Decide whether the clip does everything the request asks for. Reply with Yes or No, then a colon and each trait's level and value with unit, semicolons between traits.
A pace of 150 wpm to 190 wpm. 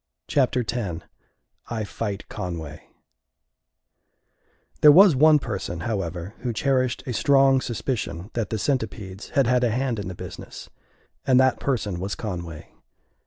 No: slow, 135 wpm